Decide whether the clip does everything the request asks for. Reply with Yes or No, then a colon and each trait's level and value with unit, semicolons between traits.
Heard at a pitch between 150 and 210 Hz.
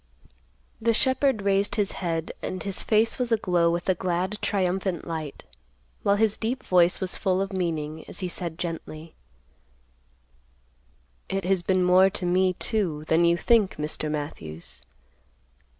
Yes: medium, 185 Hz